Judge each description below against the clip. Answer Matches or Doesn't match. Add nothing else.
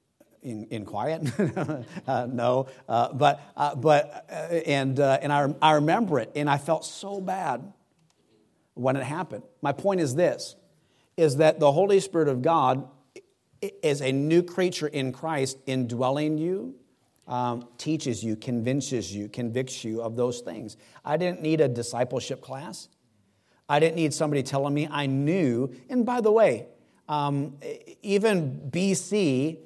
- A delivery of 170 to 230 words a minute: Doesn't match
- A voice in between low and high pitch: Matches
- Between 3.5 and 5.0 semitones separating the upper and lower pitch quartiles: Matches